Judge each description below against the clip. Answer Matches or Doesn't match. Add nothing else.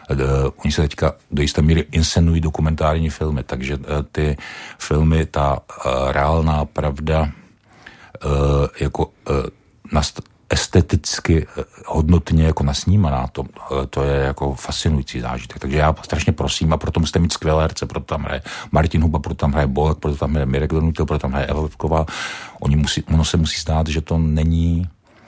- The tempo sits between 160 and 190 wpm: Matches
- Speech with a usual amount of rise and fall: Doesn't match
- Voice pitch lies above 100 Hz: Doesn't match